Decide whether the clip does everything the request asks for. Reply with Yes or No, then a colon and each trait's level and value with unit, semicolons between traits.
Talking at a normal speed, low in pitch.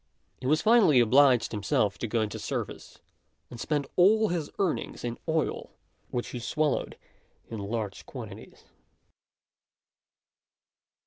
No: slow, 120 wpm; low, 130 Hz